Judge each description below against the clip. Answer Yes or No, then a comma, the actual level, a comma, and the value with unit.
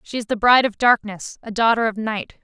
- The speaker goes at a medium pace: No, fast, 245 wpm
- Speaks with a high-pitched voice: Yes, high, 220 Hz